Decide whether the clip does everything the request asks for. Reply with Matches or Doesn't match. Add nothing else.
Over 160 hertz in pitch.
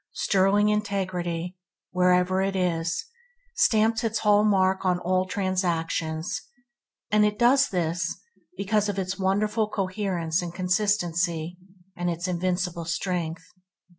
Matches